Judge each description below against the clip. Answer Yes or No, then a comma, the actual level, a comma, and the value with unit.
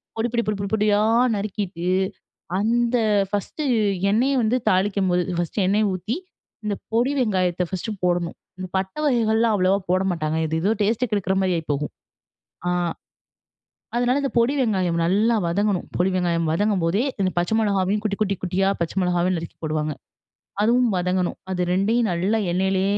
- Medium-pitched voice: No, high, 195 Hz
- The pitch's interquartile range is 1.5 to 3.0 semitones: No, average, 3.5 semitones